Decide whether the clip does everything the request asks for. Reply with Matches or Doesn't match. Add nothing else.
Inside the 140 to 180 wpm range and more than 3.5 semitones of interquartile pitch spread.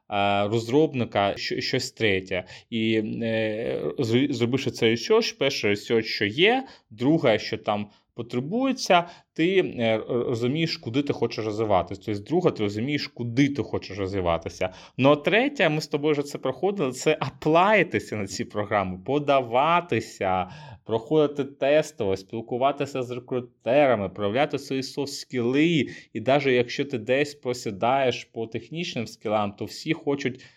Doesn't match